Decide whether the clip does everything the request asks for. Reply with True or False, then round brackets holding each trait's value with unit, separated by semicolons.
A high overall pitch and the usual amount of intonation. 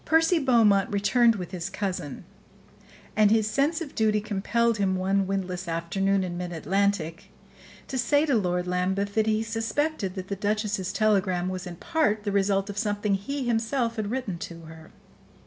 True (200 Hz; 3.3 semitones)